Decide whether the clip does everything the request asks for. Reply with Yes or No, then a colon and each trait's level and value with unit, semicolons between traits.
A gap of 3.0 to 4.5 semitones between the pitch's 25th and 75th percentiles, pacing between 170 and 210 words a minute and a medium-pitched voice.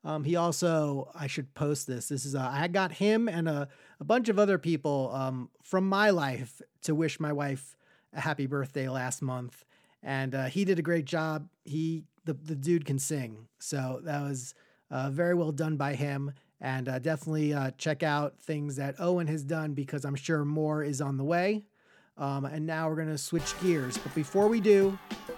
Yes: average, 3.4 semitones; average, 200 wpm; medium, 150 Hz